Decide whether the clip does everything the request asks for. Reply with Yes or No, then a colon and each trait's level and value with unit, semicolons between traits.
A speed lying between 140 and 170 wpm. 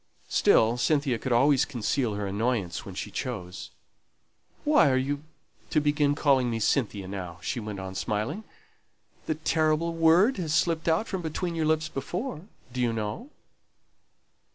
Yes: average, 155 wpm